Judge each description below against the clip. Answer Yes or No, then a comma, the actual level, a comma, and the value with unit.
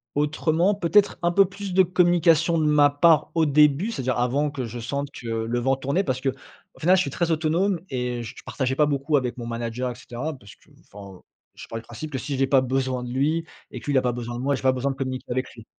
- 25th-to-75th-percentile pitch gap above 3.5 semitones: Yes, average, 4.3 semitones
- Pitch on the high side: No, medium, 140 Hz